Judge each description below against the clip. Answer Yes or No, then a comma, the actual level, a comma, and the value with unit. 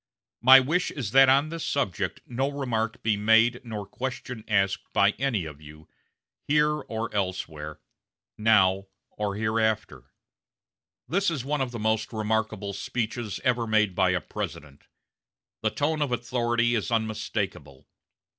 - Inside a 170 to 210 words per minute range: No, average, 140 wpm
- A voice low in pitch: Yes, low, 110 Hz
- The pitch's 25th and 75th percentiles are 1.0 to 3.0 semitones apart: No, average, 4.1 semitones